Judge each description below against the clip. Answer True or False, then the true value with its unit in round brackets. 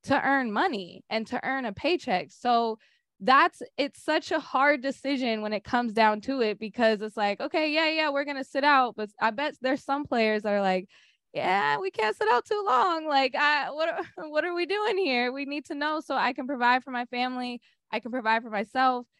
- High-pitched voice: True (260 Hz)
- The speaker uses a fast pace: True (225 wpm)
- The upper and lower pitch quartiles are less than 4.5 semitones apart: False (4.8 semitones)